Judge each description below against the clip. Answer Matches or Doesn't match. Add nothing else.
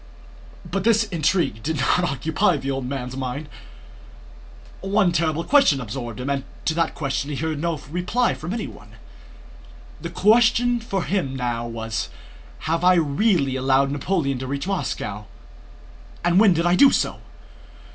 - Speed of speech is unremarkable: Matches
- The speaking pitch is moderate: Matches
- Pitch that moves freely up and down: Matches